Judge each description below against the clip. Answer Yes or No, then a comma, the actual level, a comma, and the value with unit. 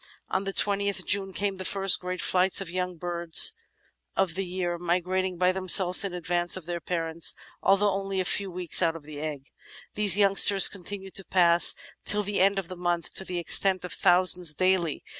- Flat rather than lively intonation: Yes, narrow, 1.9 semitones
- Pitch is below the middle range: No, medium, 185 Hz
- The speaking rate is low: No, average, 195 wpm